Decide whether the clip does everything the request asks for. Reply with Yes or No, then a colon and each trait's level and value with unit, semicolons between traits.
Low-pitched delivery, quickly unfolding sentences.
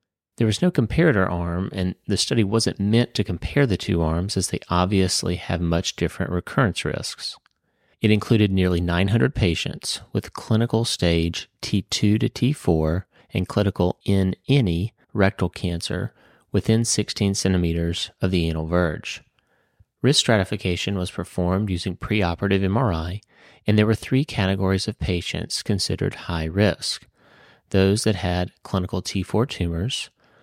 No: very low, 95 Hz; average, 140 wpm